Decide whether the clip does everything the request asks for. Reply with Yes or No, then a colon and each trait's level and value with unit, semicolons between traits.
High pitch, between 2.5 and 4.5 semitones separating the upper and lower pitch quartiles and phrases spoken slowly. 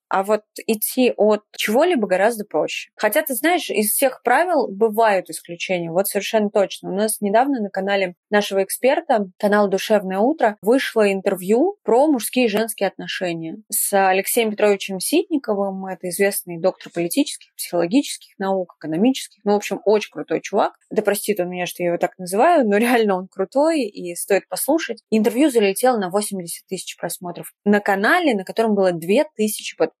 No: high, 205 Hz; average, 3.7 semitones; fast, 160 wpm